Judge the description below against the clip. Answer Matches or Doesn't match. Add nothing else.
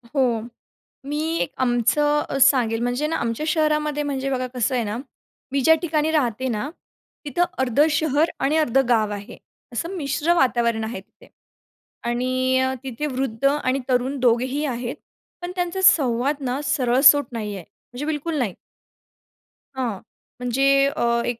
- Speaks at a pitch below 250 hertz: Doesn't match